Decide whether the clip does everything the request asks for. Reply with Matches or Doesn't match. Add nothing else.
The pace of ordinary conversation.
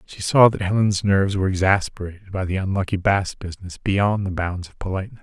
Matches